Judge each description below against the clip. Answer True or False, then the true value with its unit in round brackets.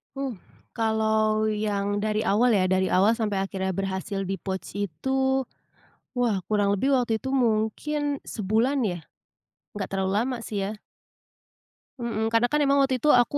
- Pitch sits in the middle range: False (215 Hz)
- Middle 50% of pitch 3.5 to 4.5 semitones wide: True (3.8 semitones)